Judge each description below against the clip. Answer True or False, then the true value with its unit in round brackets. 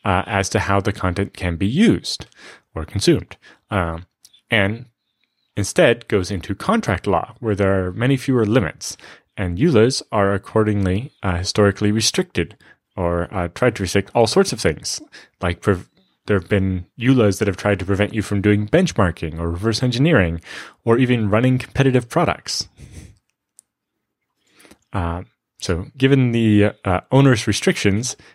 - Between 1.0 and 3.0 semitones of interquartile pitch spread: False (4.1 semitones)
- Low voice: True (105 Hz)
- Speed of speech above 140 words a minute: True (150 wpm)